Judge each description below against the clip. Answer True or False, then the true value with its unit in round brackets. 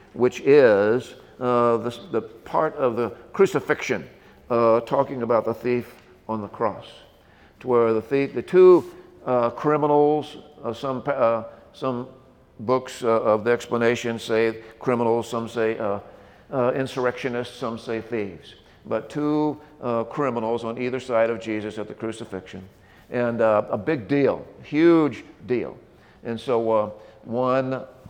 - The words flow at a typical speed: True (145 wpm)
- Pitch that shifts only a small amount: False (3.3 semitones)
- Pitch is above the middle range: False (120 Hz)